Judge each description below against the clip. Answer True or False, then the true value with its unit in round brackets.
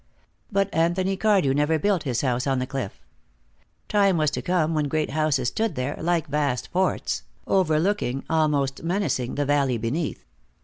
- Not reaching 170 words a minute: True (160 wpm)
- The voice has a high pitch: False (155 Hz)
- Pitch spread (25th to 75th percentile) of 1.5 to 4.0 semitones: False (4.9 semitones)